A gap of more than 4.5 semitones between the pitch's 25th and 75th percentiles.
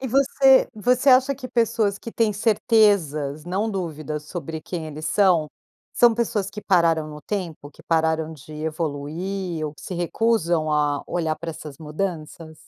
Yes: wide, 5.4 semitones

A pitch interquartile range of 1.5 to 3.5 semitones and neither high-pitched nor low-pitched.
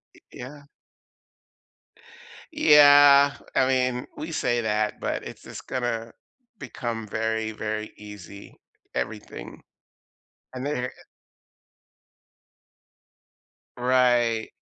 No: average, 3.0 semitones; low, 120 Hz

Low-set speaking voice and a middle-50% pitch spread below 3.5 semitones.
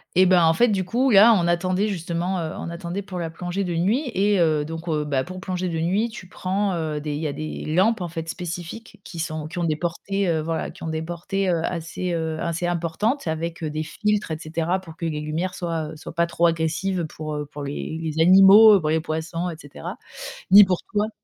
No: medium, 170 Hz; average, 2.9 semitones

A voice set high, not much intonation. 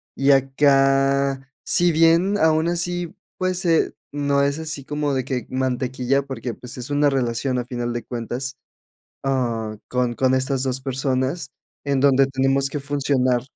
No: low, 135 Hz; narrow, 2.0 semitones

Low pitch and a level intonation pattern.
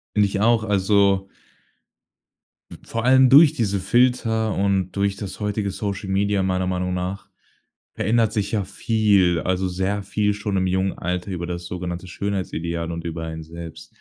Yes: very low, 95 Hz; narrow, 2.3 semitones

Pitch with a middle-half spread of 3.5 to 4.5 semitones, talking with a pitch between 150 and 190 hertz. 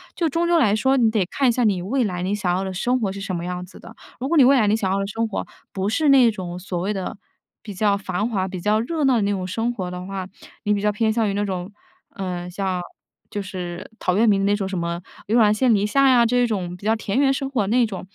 No: average, 3.8 semitones; high, 205 Hz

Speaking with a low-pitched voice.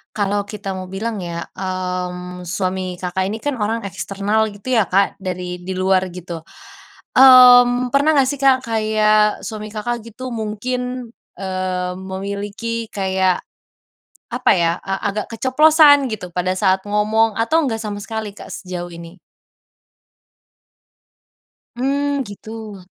No: high, 210 Hz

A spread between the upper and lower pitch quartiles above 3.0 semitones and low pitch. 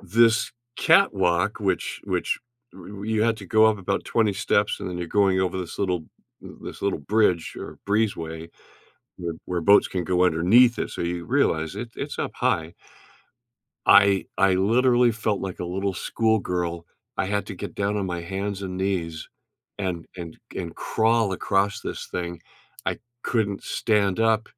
Yes: average, 3.4 semitones; very low, 95 Hz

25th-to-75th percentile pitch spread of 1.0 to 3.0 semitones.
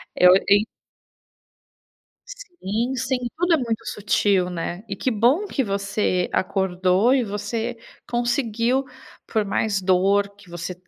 No: average, 4.3 semitones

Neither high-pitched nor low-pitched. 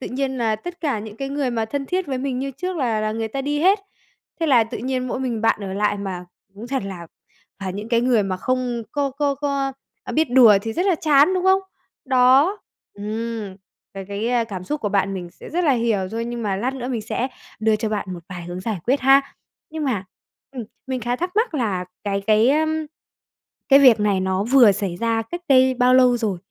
No: high, 240 Hz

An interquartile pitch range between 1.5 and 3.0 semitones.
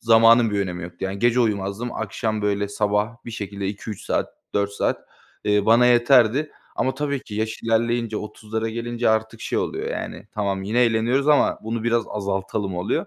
Yes: narrow, 2.5 semitones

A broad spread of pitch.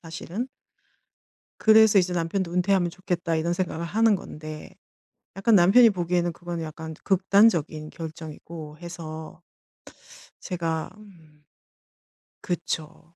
No: average, 3.0 semitones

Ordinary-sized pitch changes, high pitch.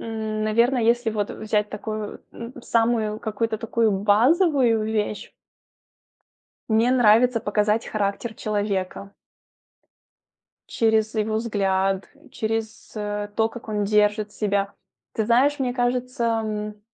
No: narrow, 1.8 semitones; high, 220 Hz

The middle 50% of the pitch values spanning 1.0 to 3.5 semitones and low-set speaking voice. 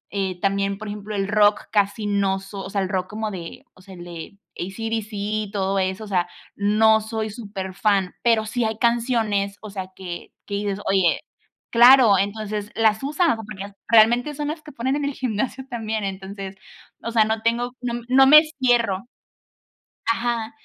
No: average, 2.8 semitones; high, 215 Hz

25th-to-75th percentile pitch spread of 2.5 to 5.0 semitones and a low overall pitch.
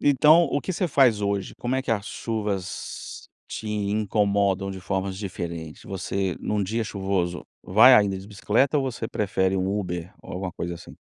Yes: average, 2.9 semitones; low, 100 Hz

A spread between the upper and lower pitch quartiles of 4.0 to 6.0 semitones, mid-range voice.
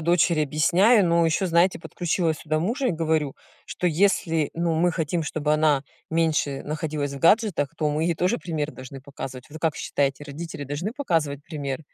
No: average, 2.8 semitones; medium, 160 Hz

